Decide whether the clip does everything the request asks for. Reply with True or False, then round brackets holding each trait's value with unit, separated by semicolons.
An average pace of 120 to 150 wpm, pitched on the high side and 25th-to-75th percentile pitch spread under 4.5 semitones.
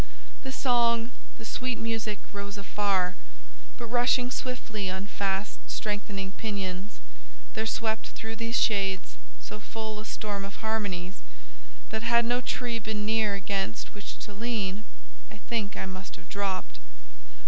True (135 wpm; 210 Hz; 2.8 semitones)